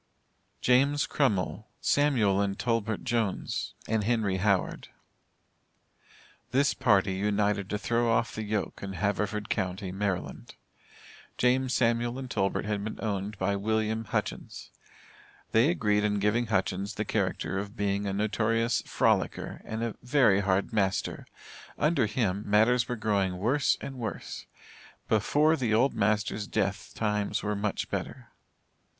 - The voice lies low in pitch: Yes, low, 105 Hz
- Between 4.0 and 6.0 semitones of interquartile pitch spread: No, average, 2.8 semitones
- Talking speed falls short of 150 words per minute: Yes, slow, 135 wpm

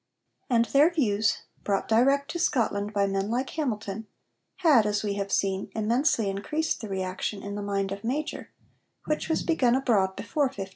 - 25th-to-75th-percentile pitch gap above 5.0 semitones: Yes, wide, 5.5 semitones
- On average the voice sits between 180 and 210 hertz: No, high, 220 Hz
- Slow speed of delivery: No, average, 175 wpm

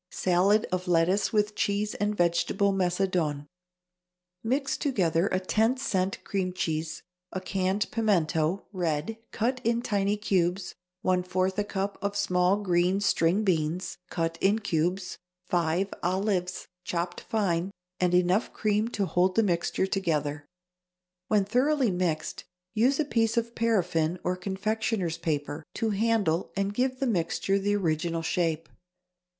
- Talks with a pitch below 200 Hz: Yes, high, 190 Hz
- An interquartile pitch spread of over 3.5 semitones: No, average, 3.2 semitones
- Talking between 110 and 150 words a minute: Yes, slow, 135 wpm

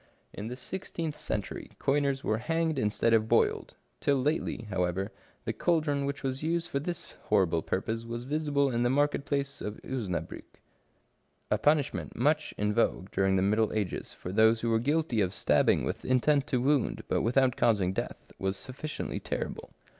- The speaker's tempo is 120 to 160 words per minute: No, average, 170 wpm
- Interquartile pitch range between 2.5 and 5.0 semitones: No, wide, 5.4 semitones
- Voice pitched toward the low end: Yes, low, 125 Hz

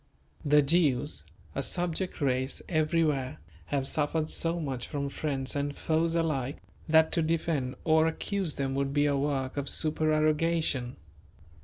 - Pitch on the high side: No, medium, 150 Hz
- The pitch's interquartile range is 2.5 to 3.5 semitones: Yes, average, 2.8 semitones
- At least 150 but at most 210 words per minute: No, average, 140 wpm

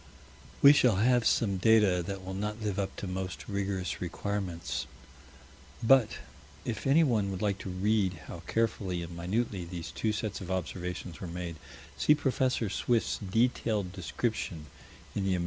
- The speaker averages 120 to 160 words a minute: Yes, average, 155 wpm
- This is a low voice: Yes, low, 100 Hz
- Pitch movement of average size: Yes, average, 3.6 semitones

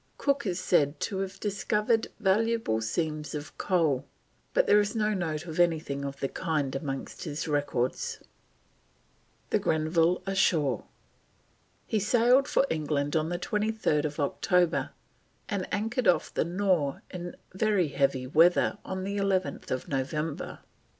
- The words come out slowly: Yes, slow, 130 wpm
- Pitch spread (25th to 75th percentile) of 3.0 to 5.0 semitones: No, wide, 5.4 semitones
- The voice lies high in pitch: No, medium, 175 Hz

